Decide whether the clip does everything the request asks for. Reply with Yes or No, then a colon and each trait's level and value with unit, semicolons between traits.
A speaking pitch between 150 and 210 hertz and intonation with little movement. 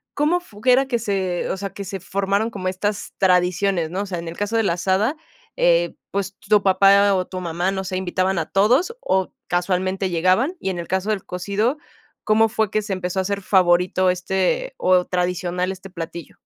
Yes: high, 190 Hz; narrow, 2.2 semitones